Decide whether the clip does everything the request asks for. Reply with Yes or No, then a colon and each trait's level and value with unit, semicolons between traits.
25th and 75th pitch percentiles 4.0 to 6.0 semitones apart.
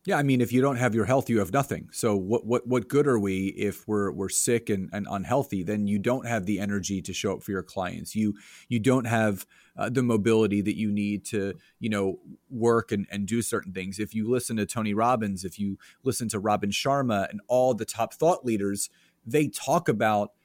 No: average, 3.4 semitones